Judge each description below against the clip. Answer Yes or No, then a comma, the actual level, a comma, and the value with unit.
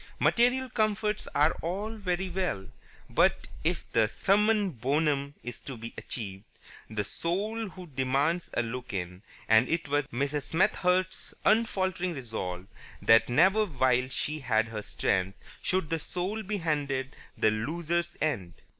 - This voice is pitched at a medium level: Yes, medium, 150 Hz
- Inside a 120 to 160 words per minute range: Yes, average, 140 wpm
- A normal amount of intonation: No, wide, 7.5 semitones